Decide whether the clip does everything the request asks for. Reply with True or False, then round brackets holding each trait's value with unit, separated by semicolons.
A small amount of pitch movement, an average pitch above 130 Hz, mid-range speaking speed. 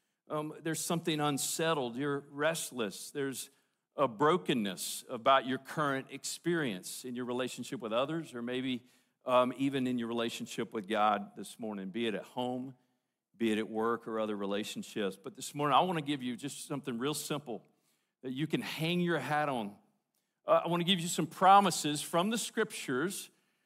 False (4.3 semitones; 140 Hz; 180 wpm)